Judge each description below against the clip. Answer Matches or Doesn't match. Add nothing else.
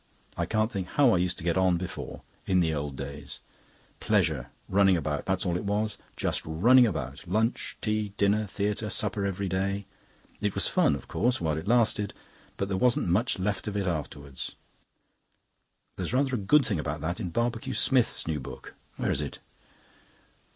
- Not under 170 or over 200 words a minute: Matches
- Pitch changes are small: Doesn't match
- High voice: Doesn't match